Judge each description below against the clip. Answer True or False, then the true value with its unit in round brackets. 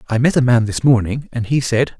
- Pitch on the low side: True (120 Hz)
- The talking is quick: True (270 wpm)